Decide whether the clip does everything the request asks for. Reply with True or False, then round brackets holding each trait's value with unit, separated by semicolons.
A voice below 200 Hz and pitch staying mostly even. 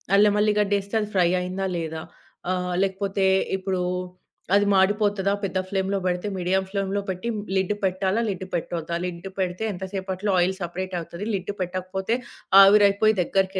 True (190 Hz; 1.7 semitones)